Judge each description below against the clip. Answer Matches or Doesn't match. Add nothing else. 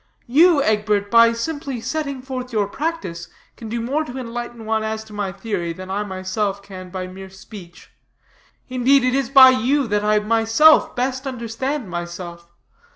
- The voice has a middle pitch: Doesn't match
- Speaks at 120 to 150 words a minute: Doesn't match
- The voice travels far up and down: Doesn't match